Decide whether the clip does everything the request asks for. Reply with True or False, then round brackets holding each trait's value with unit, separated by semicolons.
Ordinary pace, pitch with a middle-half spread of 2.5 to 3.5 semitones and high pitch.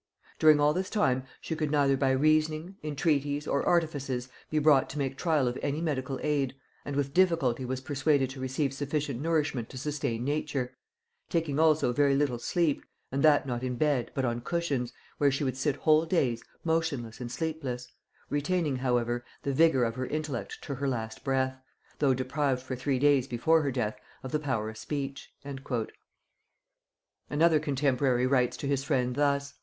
False (175 wpm; 2.9 semitones; 140 Hz)